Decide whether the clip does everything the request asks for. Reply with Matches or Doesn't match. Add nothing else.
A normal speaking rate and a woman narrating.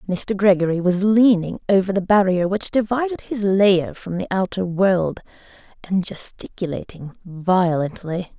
Doesn't match